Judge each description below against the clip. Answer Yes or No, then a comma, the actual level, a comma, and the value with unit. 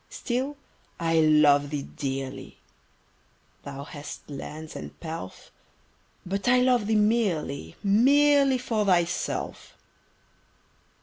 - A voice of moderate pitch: Yes, medium, 175 Hz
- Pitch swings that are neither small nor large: No, wide, 8.4 semitones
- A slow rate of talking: Yes, slow, 100 wpm